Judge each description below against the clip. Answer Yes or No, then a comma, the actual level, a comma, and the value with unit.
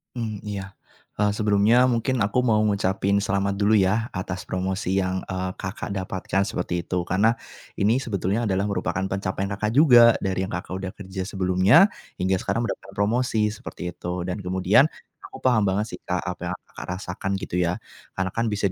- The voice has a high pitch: No, low, 100 Hz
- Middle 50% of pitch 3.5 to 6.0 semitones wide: No, narrow, 2.5 semitones